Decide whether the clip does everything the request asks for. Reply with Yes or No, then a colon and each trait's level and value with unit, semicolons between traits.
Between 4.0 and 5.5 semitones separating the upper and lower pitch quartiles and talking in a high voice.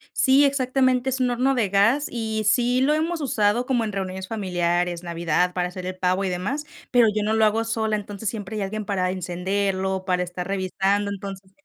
Yes: average, 4.4 semitones; high, 205 Hz